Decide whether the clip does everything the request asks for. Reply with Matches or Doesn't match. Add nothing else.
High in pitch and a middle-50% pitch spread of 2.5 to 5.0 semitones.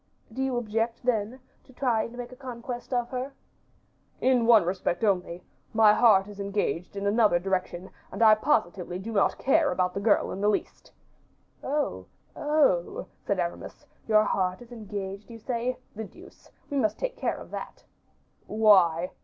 Matches